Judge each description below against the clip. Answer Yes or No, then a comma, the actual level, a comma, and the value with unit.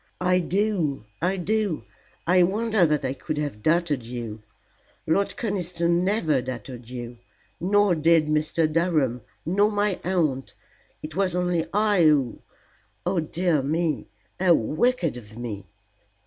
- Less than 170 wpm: Yes, slow, 135 wpm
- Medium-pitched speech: Yes, medium, 165 Hz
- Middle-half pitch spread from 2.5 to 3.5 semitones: No, wide, 5.4 semitones